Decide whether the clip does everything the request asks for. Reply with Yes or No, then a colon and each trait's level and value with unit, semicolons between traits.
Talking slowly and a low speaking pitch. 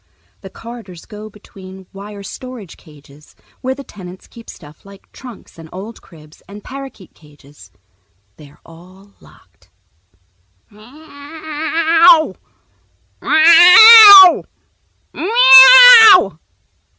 No: slow, 100 wpm; high, 225 Hz